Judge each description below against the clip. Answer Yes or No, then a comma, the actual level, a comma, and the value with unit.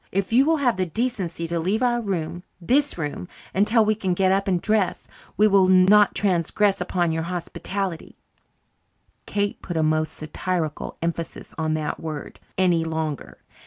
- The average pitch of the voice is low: No, medium, 185 Hz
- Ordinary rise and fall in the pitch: Yes, average, 4.1 semitones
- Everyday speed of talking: Yes, average, 165 wpm